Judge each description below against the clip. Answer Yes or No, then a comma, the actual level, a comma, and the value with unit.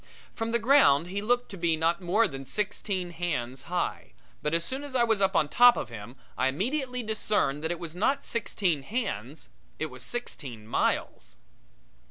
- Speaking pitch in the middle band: Yes, medium, 180 Hz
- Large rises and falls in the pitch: Yes, wide, 7.9 semitones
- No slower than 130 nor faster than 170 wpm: No, average, 185 wpm